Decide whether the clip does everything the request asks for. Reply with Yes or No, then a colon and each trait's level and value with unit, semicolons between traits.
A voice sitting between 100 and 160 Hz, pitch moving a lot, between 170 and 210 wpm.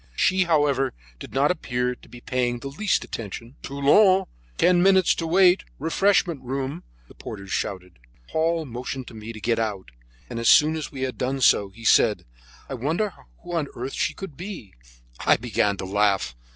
Yes: low, 135 Hz; wide, 6.4 semitones; average, 180 wpm